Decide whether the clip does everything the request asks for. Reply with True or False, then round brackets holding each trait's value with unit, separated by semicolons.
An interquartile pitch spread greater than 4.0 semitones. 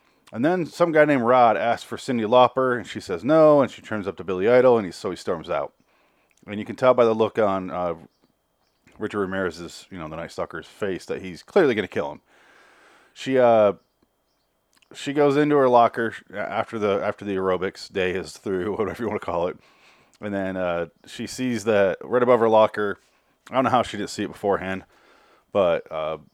True (4.6 semitones)